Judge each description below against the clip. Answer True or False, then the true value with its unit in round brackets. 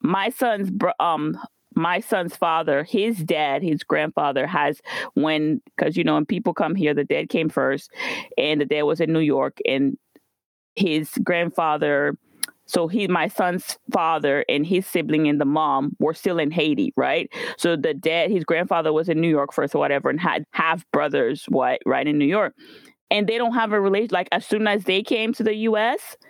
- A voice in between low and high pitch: True (170 Hz)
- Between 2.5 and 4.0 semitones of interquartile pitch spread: False (5.3 semitones)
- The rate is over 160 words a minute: True (195 wpm)